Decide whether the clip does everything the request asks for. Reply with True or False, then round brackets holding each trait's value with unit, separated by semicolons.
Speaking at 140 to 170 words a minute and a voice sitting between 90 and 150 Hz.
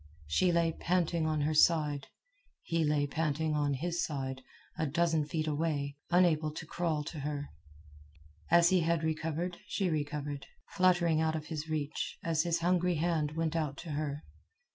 False (160 wpm; 160 Hz)